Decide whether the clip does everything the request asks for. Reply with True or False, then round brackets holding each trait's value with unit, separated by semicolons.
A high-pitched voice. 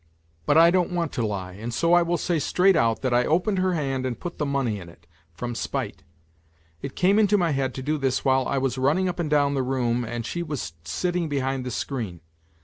False (135 Hz)